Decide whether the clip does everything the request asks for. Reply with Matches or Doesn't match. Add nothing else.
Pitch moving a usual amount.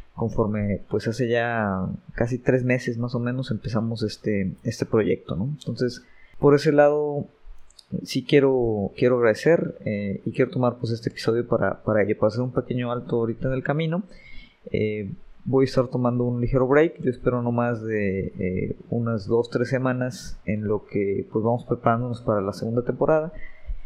Matches